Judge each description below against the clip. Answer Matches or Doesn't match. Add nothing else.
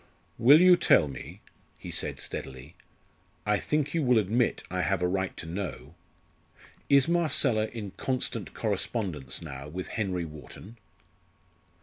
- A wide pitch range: Matches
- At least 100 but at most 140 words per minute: Matches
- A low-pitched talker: Matches